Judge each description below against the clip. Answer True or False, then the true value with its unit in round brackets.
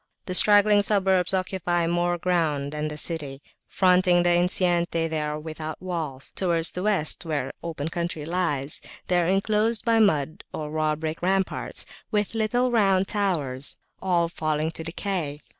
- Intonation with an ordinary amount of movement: True (3.5 semitones)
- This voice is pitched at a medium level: True (175 Hz)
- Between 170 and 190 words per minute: False (155 wpm)